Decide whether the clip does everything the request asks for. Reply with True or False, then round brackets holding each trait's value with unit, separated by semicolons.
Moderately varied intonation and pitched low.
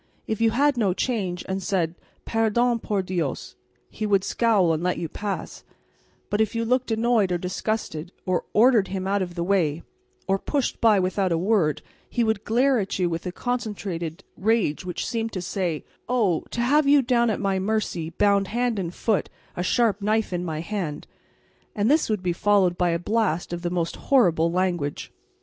False (4.2 semitones; 195 Hz)